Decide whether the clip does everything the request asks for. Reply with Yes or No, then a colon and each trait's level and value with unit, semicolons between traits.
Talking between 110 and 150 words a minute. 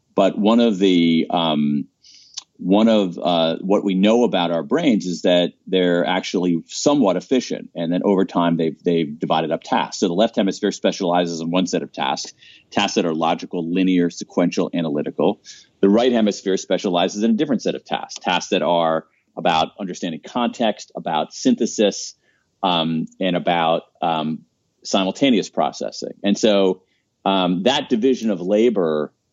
No: average, 160 wpm